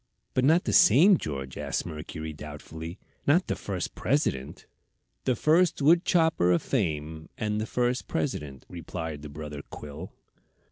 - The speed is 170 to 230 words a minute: No, average, 145 wpm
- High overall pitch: No, very low, 90 Hz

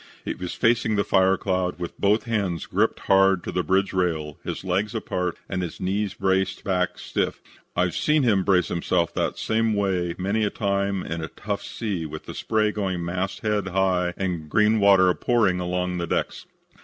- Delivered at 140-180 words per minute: No, average, 190 wpm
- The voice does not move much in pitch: Yes, narrow, 2.3 semitones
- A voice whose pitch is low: Yes, very low, 95 Hz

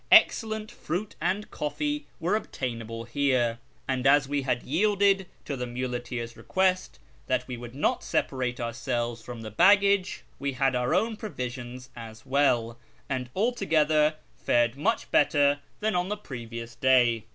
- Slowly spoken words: No, average, 145 wpm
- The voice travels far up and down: Yes, wide, 7.3 semitones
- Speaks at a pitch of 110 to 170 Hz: Yes, low, 135 Hz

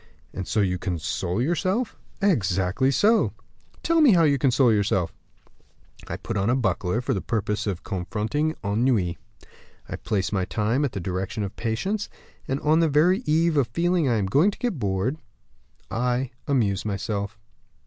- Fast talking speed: No, average, 165 wpm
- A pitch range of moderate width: No, wide, 7.3 semitones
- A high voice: No, low, 115 Hz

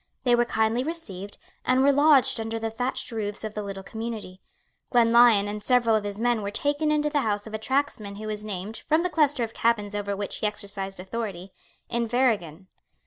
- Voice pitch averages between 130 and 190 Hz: No, high, 220 Hz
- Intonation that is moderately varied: Yes, average, 3.3 semitones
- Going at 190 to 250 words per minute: Yes, average, 200 wpm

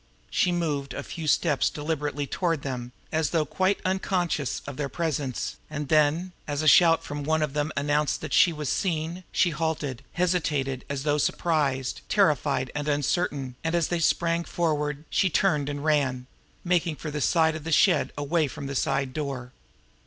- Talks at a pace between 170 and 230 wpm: Yes, average, 175 wpm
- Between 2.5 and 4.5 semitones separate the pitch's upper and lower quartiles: Yes, average, 2.8 semitones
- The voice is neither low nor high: Yes, medium, 150 Hz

